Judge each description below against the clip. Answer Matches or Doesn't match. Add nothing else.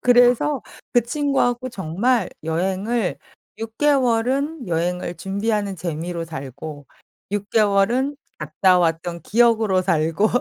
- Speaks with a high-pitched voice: Matches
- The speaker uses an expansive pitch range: Matches